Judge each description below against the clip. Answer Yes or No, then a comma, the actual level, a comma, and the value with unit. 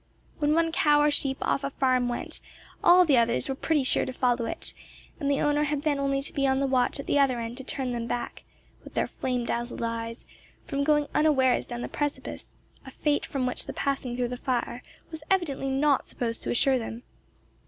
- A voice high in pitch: Yes, very high, 270 Hz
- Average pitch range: Yes, average, 3.0 semitones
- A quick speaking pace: Yes, fast, 215 wpm